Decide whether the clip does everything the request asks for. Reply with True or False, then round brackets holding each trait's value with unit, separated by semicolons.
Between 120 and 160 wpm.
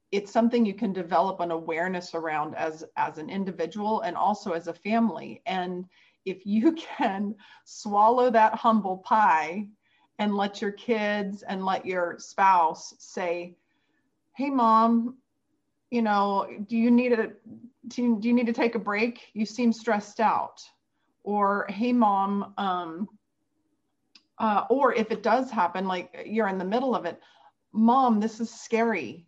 True (155 wpm)